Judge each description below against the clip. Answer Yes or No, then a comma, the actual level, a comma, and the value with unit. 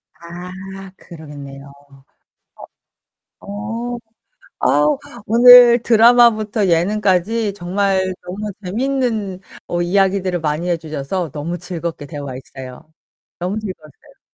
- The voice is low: No, medium, 185 Hz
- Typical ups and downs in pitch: Yes, average, 4.4 semitones